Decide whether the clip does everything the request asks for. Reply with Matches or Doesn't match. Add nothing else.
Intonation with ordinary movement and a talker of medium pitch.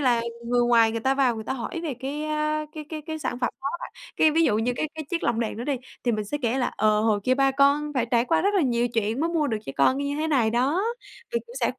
Doesn't match